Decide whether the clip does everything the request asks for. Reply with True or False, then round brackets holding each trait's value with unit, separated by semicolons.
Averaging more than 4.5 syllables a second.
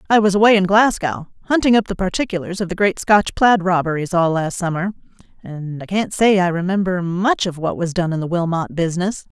True (5.6 syllables/s)